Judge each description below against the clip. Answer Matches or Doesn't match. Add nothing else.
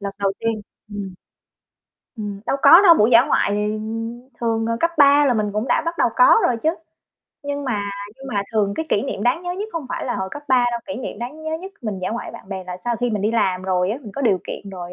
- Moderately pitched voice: Doesn't match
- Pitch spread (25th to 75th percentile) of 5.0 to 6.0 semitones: Matches